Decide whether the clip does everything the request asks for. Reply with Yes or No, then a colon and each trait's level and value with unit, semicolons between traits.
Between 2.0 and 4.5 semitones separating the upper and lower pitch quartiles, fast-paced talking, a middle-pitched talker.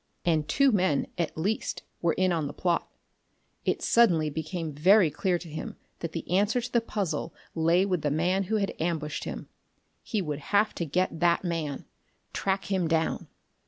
No: average, 3.4 semitones; average, 180 wpm; medium, 175 Hz